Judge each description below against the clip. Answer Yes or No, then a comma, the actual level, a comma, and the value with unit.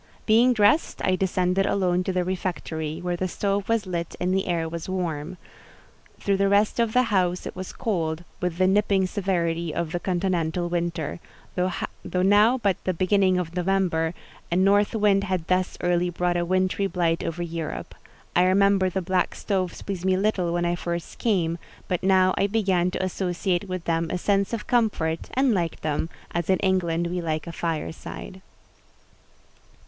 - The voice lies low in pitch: No, medium, 185 Hz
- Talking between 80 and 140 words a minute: No, average, 175 wpm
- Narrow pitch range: Yes, narrow, 2.2 semitones